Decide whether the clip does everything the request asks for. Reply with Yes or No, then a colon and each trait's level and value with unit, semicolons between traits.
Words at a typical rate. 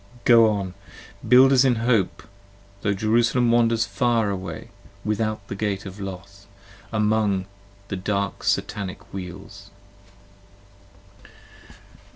No: slow, 100 wpm